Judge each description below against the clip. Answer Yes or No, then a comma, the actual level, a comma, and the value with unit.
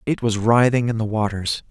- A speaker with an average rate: No, fast, 210 wpm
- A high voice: No, low, 115 Hz